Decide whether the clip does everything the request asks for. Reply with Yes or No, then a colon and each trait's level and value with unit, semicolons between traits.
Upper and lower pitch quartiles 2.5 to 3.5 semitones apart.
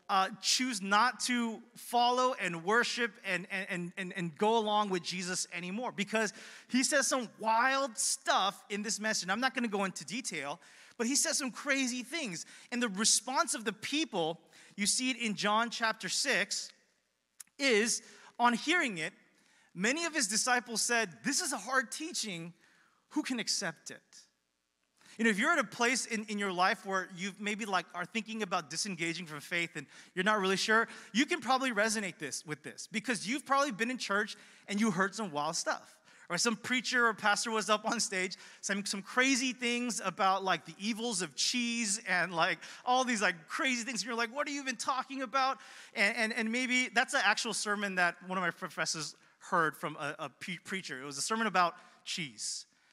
No: average, 4.8 semitones